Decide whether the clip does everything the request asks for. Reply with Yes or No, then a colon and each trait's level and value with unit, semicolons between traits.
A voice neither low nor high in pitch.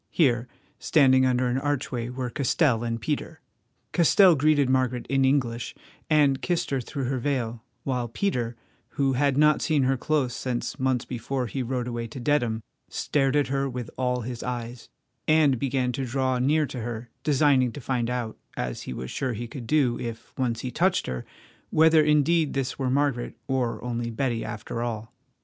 No: low, 130 Hz